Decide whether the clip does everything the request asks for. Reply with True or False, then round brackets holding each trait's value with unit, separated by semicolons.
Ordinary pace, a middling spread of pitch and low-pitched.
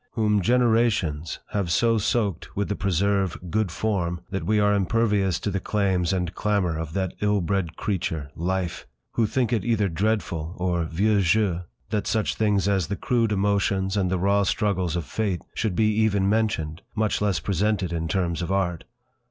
True (175 wpm; 3.2 semitones; 100 Hz)